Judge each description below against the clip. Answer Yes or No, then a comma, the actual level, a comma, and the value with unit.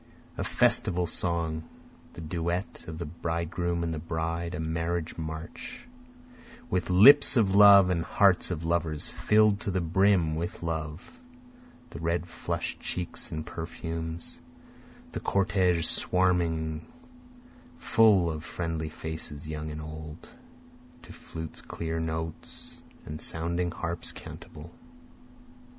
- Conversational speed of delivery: No, slow, 120 wpm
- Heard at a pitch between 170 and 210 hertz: No, very low, 85 Hz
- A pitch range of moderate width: No, narrow, 1.9 semitones